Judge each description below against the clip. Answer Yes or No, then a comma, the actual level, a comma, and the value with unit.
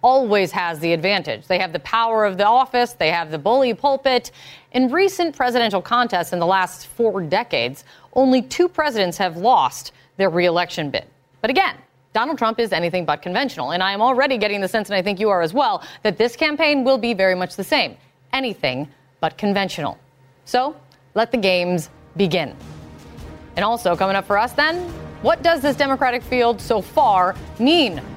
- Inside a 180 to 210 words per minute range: Yes, average, 185 wpm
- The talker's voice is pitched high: Yes, high, 205 Hz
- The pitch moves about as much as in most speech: No, wide, 6.2 semitones